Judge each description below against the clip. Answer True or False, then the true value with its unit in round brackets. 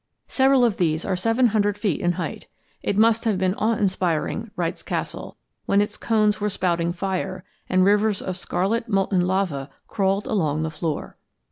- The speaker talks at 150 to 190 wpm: True (170 wpm)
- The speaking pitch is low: False (195 Hz)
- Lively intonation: False (3.1 semitones)